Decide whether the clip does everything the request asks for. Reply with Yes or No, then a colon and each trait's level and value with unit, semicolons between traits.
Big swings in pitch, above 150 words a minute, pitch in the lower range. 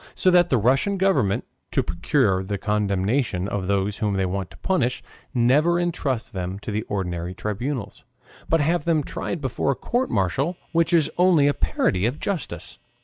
Yes: wide, 8.7 semitones; average, 175 wpm; low, 120 Hz